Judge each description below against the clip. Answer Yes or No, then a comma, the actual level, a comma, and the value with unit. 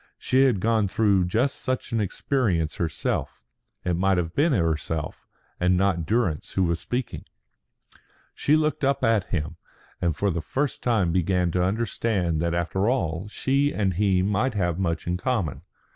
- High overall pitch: No, very low, 95 Hz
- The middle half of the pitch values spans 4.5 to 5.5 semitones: Yes, average, 5.2 semitones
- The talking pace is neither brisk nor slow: Yes, average, 165 wpm